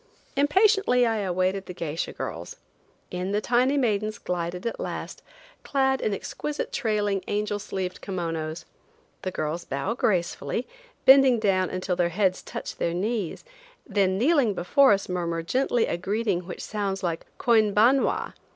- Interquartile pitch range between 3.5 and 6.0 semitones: Yes, average, 4.6 semitones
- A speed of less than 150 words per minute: Yes, average, 140 wpm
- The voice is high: Yes, high, 200 Hz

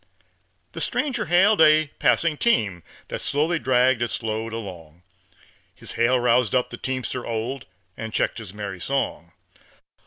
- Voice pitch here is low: Yes, low, 120 Hz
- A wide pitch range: No, average, 4.7 semitones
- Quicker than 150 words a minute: No, average, 145 wpm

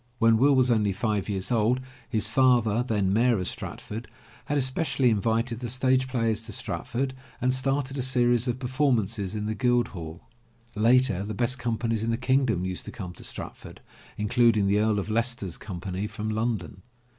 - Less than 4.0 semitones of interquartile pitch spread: Yes, average, 3.2 semitones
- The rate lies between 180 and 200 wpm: Yes, average, 190 wpm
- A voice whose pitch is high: No, low, 115 Hz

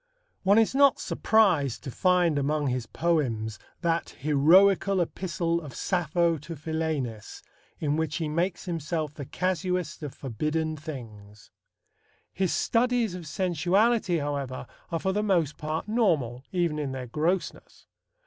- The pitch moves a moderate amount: Yes, average, 4.2 semitones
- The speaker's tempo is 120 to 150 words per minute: Yes, slow, 135 wpm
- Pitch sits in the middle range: Yes, medium, 160 Hz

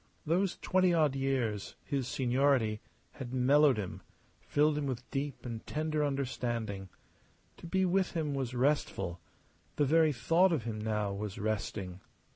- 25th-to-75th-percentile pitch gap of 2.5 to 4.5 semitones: No, wide, 5.4 semitones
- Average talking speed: Yes, average, 145 wpm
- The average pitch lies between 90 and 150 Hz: Yes, low, 135 Hz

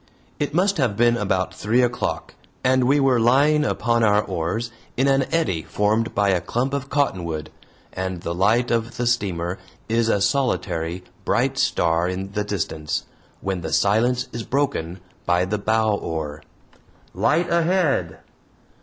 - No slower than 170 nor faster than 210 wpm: No, average, 155 wpm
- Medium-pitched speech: No, low, 110 Hz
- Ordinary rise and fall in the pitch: No, wide, 5.8 semitones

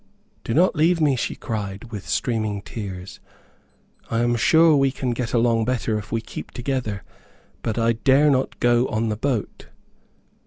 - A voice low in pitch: Yes, low, 120 Hz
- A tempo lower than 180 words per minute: Yes, average, 165 wpm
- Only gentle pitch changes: No, average, 3.4 semitones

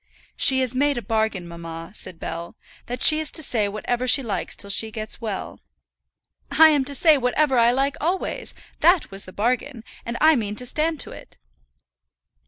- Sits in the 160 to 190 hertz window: No, high, 245 Hz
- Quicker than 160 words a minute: Yes, average, 190 wpm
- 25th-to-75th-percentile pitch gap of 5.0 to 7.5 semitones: Yes, wide, 5.4 semitones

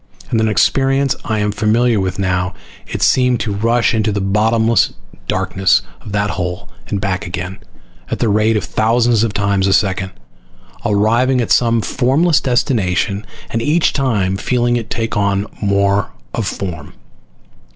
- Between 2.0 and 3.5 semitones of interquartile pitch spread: Yes, average, 3.2 semitones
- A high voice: No, low, 105 Hz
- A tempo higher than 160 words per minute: No, average, 155 wpm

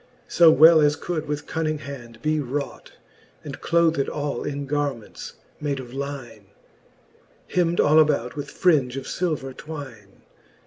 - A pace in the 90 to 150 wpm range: Yes, average, 140 wpm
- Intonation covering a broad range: No, average, 2.8 semitones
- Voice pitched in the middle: Yes, medium, 145 Hz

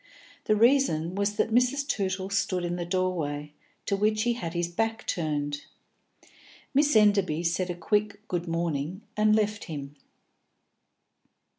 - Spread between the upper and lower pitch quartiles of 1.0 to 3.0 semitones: No, average, 4.1 semitones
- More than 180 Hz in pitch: Yes, high, 190 Hz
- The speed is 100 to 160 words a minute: Yes, average, 140 wpm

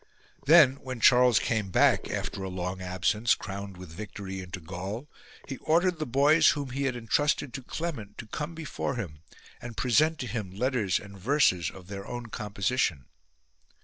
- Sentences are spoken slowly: No, average, 175 wpm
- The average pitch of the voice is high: No, low, 115 Hz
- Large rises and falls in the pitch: Yes, wide, 6.1 semitones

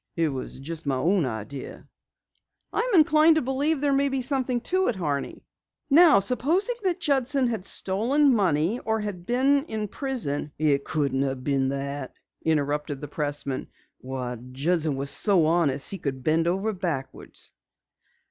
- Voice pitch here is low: No, medium, 175 Hz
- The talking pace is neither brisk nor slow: Yes, average, 155 wpm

